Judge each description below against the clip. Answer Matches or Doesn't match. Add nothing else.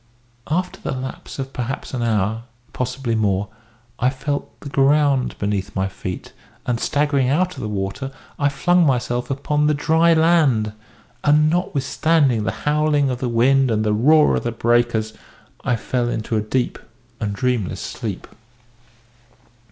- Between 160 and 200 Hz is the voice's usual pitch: Doesn't match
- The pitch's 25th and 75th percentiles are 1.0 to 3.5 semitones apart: Doesn't match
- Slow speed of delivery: Doesn't match